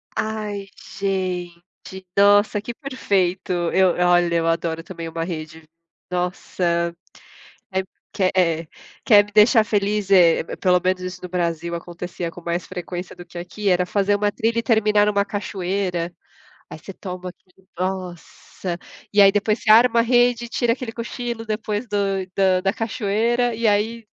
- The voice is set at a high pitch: Yes, high, 195 Hz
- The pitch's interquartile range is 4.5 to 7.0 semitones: No, average, 3.3 semitones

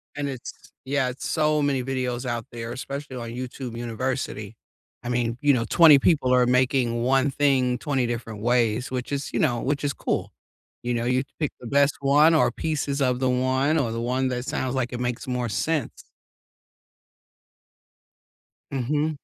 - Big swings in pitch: No, narrow, 2.5 semitones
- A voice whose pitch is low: Yes, low, 130 Hz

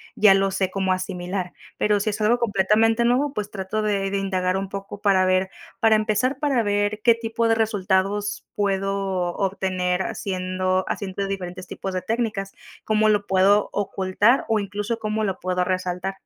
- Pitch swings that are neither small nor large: No, narrow, 2.3 semitones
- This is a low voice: No, high, 195 Hz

